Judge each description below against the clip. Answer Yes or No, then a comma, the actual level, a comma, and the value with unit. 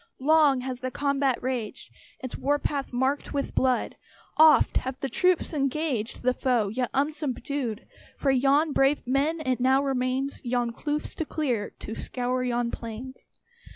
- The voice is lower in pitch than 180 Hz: No, very high, 265 Hz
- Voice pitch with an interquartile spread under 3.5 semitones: Yes, narrow, 2.4 semitones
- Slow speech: No, average, 155 wpm